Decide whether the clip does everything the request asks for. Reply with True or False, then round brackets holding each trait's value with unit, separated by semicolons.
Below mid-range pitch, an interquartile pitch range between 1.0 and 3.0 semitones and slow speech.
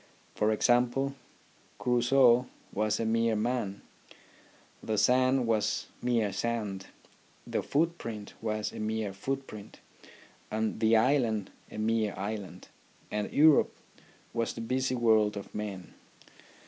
True (110 Hz; 2.6 semitones; 115 wpm)